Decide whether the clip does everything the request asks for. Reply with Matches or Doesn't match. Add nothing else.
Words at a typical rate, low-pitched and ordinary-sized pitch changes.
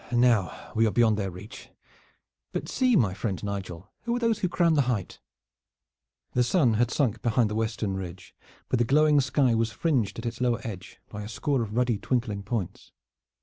Matches